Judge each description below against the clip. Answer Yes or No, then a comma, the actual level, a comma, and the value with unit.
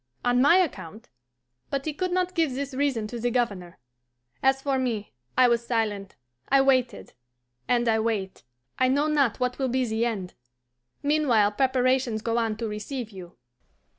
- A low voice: No, high, 245 Hz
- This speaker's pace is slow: No, average, 165 wpm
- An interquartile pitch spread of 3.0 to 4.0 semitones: Yes, average, 3.6 semitones